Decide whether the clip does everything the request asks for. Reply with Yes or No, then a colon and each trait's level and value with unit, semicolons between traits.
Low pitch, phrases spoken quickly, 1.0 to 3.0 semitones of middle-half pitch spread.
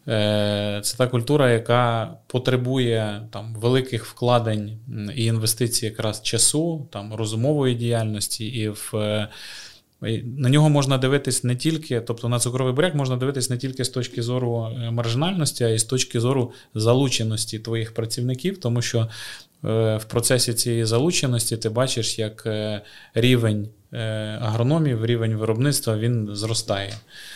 No: low, 120 Hz; average, 125 wpm; narrow, 2.5 semitones